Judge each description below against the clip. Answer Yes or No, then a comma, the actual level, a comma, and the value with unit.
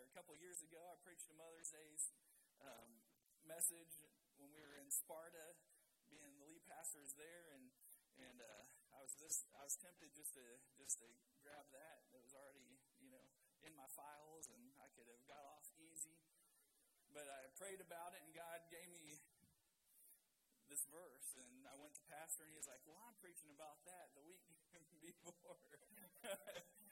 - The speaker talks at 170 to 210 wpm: Yes, average, 180 wpm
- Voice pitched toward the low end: No, medium, 160 Hz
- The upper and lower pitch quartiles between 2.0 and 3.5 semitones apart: Yes, average, 2.8 semitones